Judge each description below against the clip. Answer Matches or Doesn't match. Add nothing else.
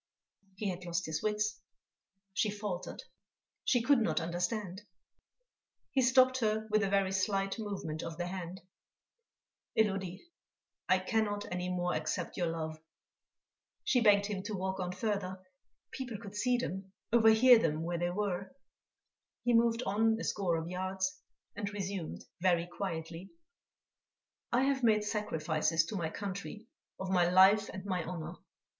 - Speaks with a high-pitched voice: Matches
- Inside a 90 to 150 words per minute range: Matches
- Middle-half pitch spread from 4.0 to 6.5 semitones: Doesn't match